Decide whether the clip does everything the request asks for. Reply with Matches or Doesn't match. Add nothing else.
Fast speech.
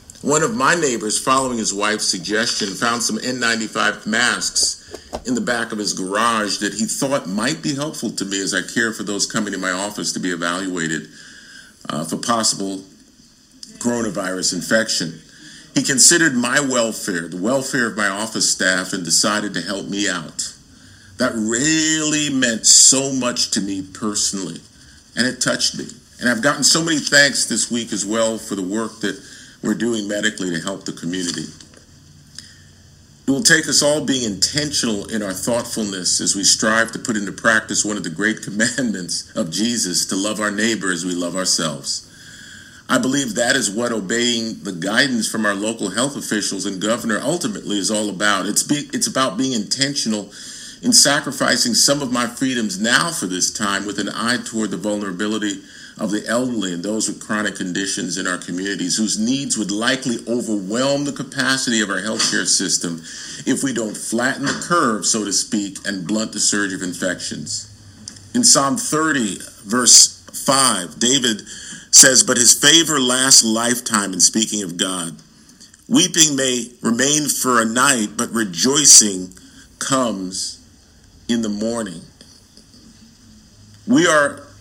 Doesn't match